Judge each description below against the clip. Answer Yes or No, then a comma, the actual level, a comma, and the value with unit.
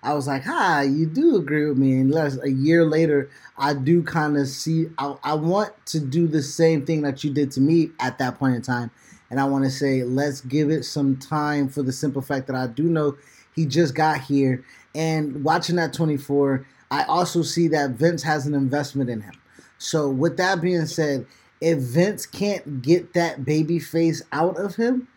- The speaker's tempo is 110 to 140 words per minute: No, fast, 205 wpm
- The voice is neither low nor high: Yes, medium, 150 Hz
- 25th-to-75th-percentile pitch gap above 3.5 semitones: No, average, 3.1 semitones